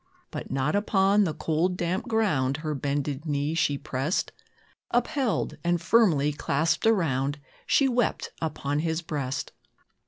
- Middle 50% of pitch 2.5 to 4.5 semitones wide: No, average, 5.2 semitones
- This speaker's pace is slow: Yes, slow, 130 wpm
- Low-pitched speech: No, medium, 160 Hz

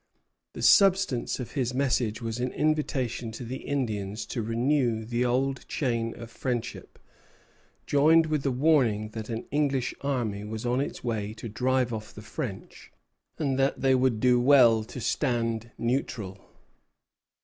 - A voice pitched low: Yes, low, 125 Hz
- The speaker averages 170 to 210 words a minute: No, average, 150 wpm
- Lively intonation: No, average, 3.1 semitones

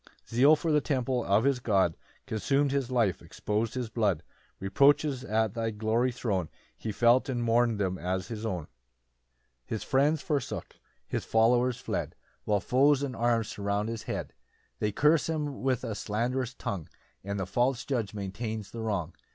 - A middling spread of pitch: Yes, average, 3.8 semitones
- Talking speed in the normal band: Yes, average, 175 wpm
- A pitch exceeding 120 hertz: No, low, 115 Hz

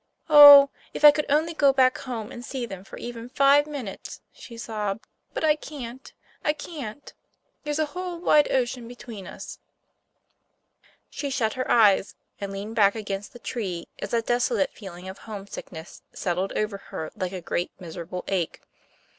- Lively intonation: Yes, wide, 6.1 semitones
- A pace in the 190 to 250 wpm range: No, average, 165 wpm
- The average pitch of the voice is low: No, high, 235 Hz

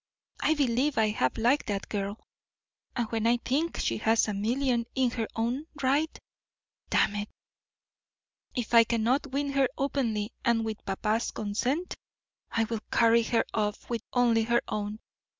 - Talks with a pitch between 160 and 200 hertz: No, high, 230 Hz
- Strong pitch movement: No, average, 3.3 semitones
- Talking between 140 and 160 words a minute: Yes, average, 155 wpm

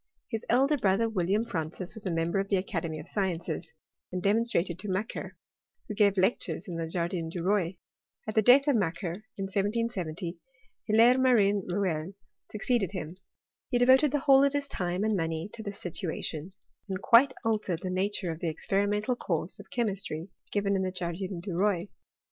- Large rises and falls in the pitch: No, average, 4.0 semitones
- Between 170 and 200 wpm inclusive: Yes, average, 180 wpm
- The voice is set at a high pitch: Yes, high, 195 Hz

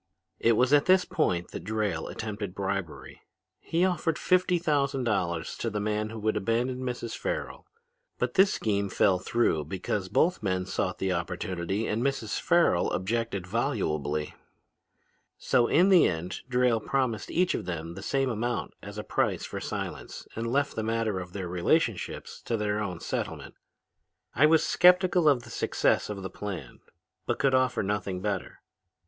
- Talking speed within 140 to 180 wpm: Yes, average, 165 wpm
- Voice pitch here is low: Yes, low, 110 Hz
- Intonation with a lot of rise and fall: Yes, wide, 6.1 semitones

